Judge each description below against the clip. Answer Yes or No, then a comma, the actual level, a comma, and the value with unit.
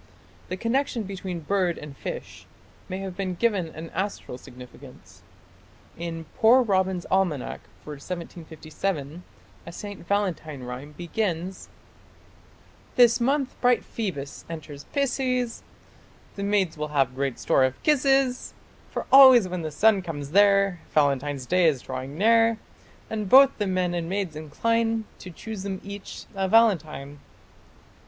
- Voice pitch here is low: No, medium, 185 Hz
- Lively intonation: Yes, wide, 6.2 semitones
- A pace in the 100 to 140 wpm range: Yes, slow, 135 wpm